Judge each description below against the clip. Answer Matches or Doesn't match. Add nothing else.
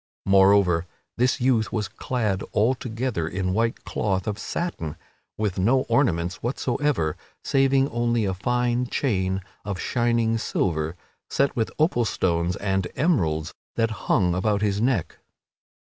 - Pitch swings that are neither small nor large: Matches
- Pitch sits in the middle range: Doesn't match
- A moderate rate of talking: Doesn't match